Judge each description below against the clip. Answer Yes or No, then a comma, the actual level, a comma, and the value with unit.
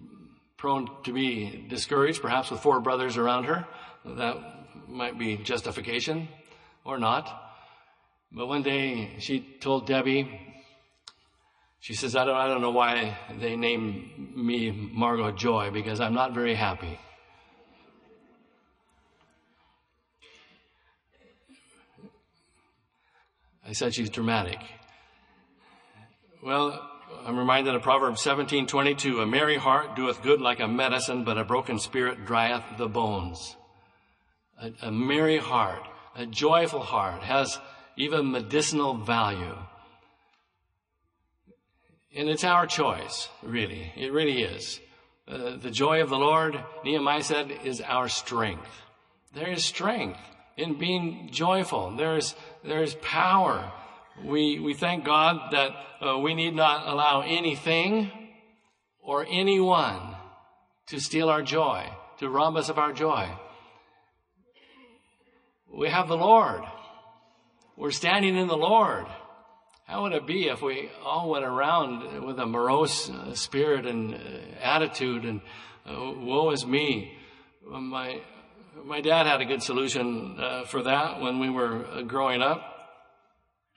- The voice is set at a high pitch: No, low, 135 Hz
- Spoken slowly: Yes, slow, 125 wpm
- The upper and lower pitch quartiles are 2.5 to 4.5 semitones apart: No, average, 4.9 semitones